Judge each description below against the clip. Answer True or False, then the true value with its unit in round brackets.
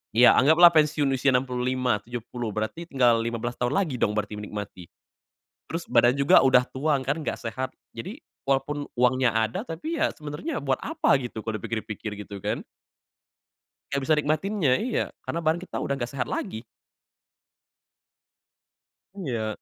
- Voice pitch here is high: False (130 Hz)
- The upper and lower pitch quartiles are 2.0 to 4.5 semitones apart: False (5.0 semitones)